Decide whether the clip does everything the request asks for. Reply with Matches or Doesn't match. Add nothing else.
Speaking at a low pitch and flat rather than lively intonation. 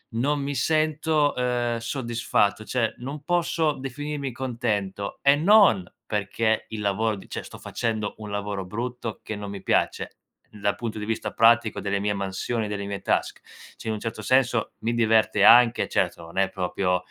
Doesn't match